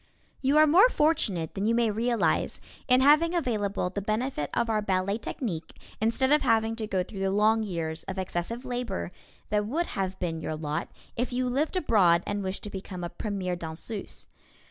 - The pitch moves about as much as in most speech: Yes, average, 5.0 semitones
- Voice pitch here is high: Yes, high, 210 Hz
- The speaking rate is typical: Yes, average, 190 wpm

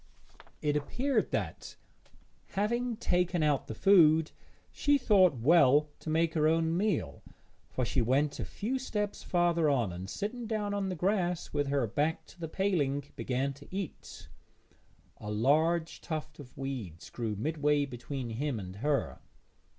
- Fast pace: No, average, 150 wpm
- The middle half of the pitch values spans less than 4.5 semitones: No, average, 5.3 semitones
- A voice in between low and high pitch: Yes, medium, 155 Hz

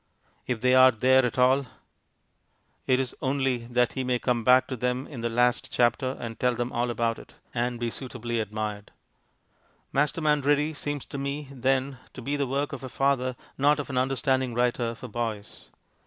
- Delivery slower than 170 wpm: No, average, 185 wpm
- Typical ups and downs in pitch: No, narrow, 2.2 semitones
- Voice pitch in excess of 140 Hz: No, low, 125 Hz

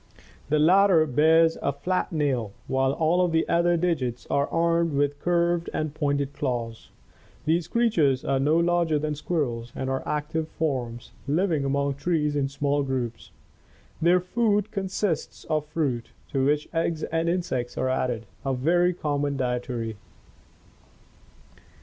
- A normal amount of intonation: Yes, average, 4.0 semitones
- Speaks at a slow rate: No, average, 150 wpm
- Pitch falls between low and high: Yes, medium, 150 Hz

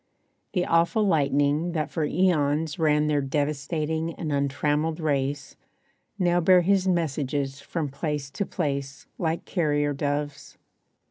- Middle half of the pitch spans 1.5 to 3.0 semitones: Yes, average, 2.7 semitones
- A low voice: No, medium, 150 Hz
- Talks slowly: Yes, slow, 125 wpm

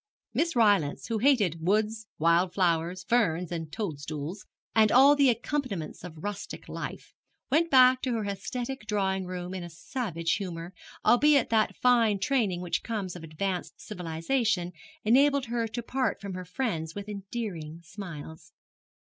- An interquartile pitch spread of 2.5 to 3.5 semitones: No, wide, 5.6 semitones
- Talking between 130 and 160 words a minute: Yes, average, 145 wpm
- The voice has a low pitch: No, high, 200 Hz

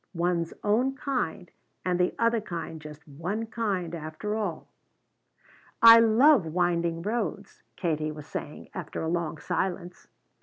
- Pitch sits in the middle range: Yes, medium, 180 Hz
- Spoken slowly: Yes, slow, 130 wpm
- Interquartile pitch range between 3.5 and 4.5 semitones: No, average, 4.9 semitones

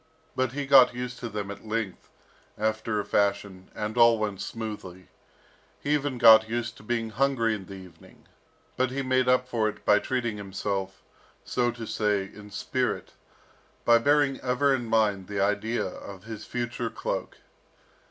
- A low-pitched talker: Yes, low, 110 Hz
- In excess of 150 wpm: Yes, average, 165 wpm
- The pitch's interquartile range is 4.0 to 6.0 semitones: No, average, 3.3 semitones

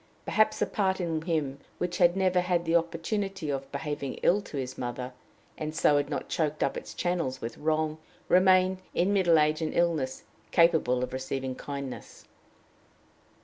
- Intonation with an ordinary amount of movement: Yes, average, 4.3 semitones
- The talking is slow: No, average, 165 wpm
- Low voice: No, medium, 160 Hz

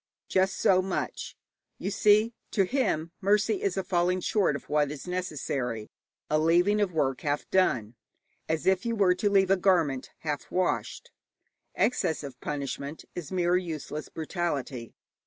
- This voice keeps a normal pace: Yes, average, 155 wpm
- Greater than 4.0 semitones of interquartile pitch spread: Yes, average, 4.6 semitones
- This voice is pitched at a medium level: Yes, medium, 175 Hz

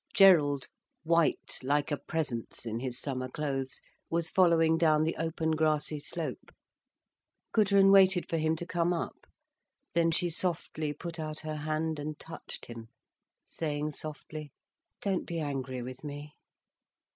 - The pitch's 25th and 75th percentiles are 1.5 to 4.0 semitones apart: Yes, narrow, 2.4 semitones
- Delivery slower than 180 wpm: Yes, average, 140 wpm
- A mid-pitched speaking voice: Yes, medium, 155 Hz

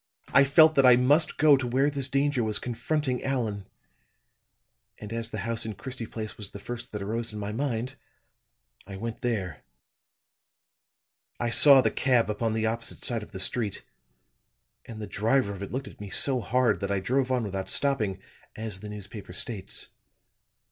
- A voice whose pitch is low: Yes, low, 115 Hz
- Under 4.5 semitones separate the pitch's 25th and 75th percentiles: Yes, average, 3.9 semitones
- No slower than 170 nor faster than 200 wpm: Yes, average, 180 wpm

